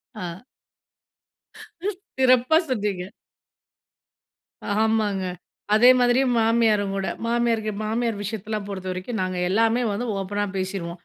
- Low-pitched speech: No, high, 215 Hz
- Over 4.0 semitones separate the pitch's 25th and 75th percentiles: No, average, 3.2 semitones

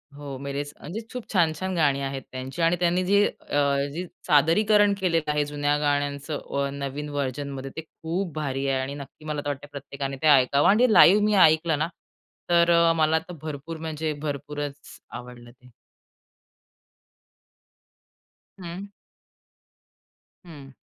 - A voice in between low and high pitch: Yes, medium, 150 Hz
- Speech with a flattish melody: No, average, 3.2 semitones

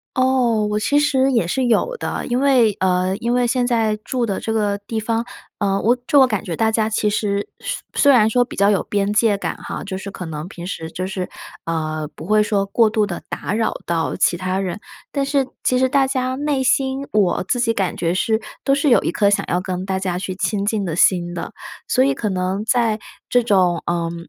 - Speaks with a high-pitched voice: Yes, high, 215 Hz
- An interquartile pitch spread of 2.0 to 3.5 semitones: No, average, 4.8 semitones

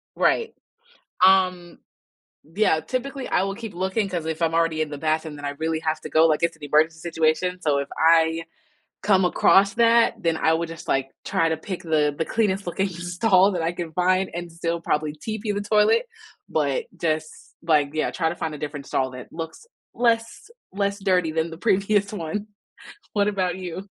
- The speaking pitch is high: No, medium, 170 Hz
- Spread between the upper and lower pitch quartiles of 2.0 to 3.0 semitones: No, average, 3.7 semitones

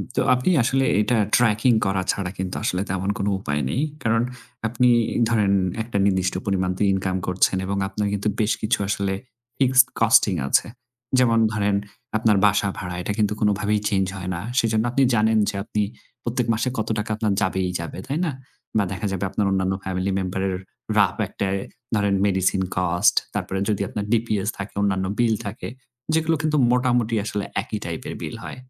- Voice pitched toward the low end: Yes, low, 105 Hz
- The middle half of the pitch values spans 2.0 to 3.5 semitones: Yes, average, 2.9 semitones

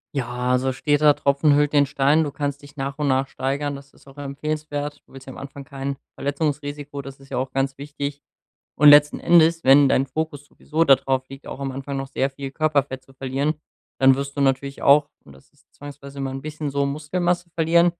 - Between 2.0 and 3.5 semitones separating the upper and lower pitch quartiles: No, narrow, 1.5 semitones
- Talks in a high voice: No, medium, 140 Hz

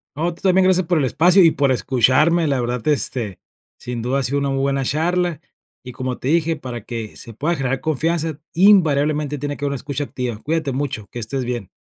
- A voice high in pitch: No, medium, 140 Hz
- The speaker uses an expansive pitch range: No, average, 4.3 semitones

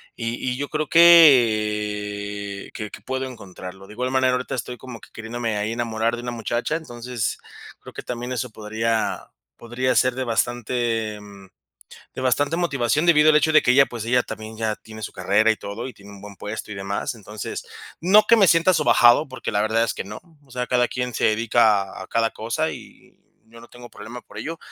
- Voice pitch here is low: Yes, low, 120 Hz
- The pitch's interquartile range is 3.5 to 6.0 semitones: No, average, 3.0 semitones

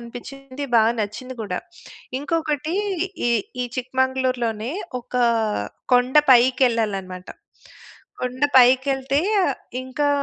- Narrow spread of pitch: Yes, narrow, 2.3 semitones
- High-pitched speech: Yes, very high, 255 Hz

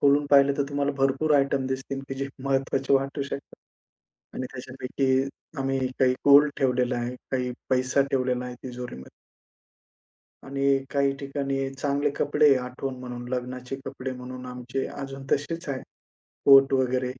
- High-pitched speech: No, low, 135 Hz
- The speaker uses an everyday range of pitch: No, narrow, 1.5 semitones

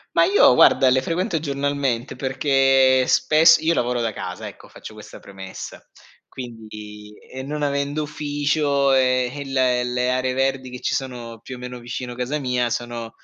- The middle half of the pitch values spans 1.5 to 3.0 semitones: Yes, narrow, 2.5 semitones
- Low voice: Yes, low, 130 Hz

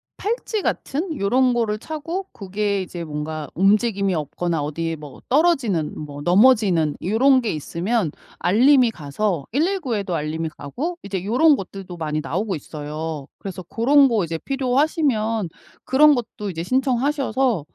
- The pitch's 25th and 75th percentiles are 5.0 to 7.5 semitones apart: No, wide, 8.0 semitones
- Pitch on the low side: No, high, 210 Hz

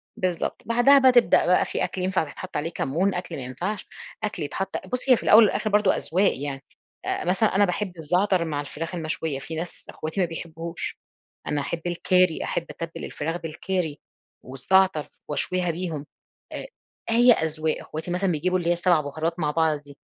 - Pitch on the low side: No, medium, 170 Hz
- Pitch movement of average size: Yes, average, 3.3 semitones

